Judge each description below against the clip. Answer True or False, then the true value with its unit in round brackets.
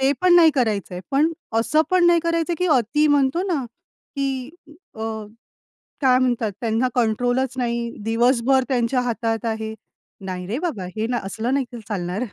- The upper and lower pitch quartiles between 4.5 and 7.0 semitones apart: False (3.7 semitones)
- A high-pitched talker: True (245 Hz)